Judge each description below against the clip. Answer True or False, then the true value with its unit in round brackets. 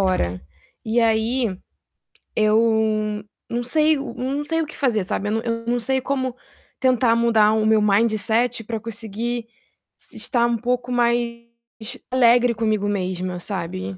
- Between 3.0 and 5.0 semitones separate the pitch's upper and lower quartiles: False (2.4 semitones)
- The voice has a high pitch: True (230 Hz)